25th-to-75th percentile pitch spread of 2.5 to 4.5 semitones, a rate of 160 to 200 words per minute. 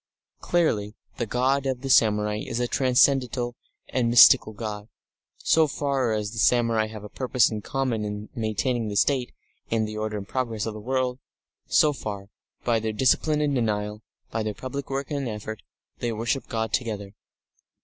Yes: average, 3.4 semitones; average, 170 wpm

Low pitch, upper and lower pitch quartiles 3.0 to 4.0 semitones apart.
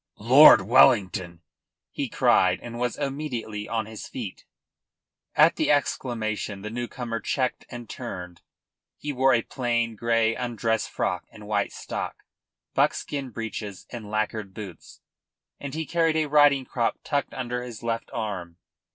Yes: low, 115 Hz; average, 3.3 semitones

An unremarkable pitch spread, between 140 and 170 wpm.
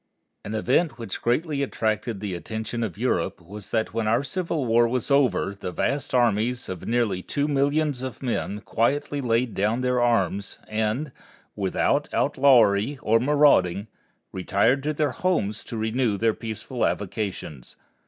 Yes: average, 4.3 semitones; average, 150 wpm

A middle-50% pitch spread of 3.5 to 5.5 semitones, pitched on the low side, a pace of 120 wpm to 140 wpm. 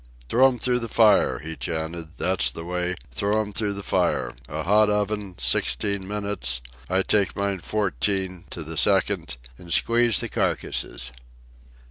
Yes: average, 4.8 semitones; very low, 95 Hz; slow, 135 wpm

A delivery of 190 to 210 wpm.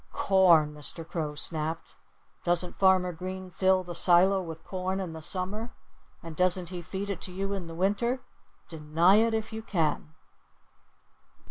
No: average, 155 wpm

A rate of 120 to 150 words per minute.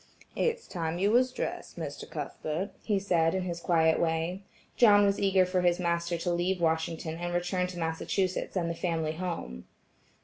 No: average, 175 wpm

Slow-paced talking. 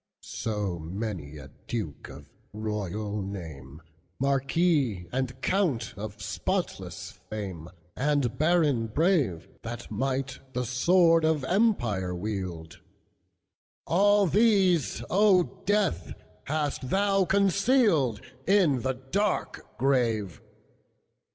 Yes: slow, 80 wpm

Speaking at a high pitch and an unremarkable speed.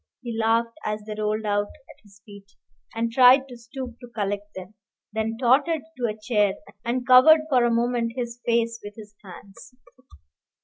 Yes: high, 230 Hz; average, 175 wpm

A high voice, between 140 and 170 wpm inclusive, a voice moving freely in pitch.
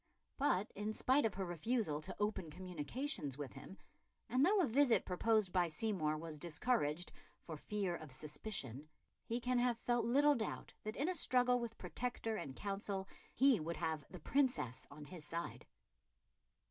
Yes: high, 195 Hz; average, 165 wpm; wide, 7.7 semitones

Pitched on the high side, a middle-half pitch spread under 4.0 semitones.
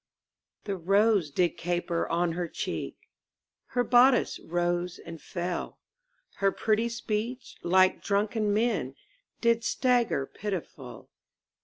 No: high, 195 Hz; average, 4.7 semitones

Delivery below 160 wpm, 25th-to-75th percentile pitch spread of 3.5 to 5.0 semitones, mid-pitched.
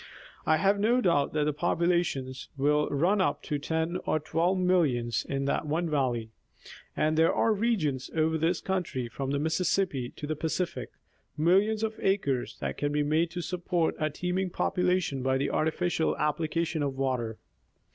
No: average, 165 wpm; average, 4.2 semitones; medium, 160 Hz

